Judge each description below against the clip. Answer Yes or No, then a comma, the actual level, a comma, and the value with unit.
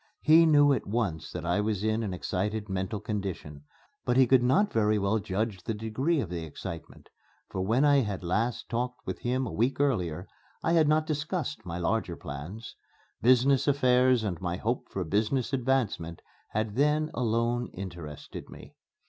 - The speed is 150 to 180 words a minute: Yes, average, 175 wpm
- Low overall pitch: Yes, low, 110 Hz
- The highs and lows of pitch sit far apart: Yes, wide, 5.7 semitones